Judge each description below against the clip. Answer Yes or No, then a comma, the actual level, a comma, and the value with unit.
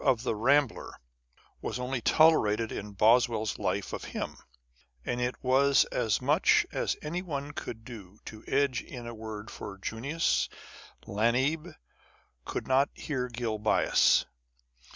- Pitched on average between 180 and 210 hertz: No, low, 125 Hz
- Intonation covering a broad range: No, average, 4.2 semitones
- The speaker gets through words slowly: Yes, slow, 130 wpm